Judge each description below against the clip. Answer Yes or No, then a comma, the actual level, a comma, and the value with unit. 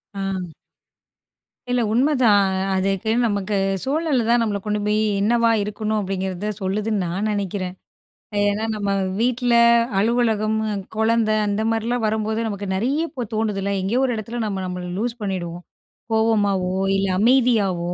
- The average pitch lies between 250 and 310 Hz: No, high, 215 Hz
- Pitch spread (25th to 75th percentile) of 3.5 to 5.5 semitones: No, average, 2.8 semitones